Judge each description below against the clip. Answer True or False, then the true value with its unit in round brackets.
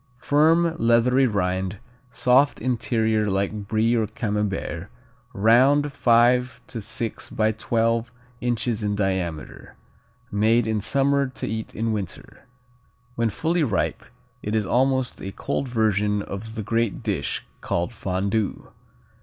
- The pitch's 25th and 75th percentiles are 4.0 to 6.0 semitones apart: False (3.2 semitones)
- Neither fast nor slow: False (125 wpm)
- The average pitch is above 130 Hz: False (110 Hz)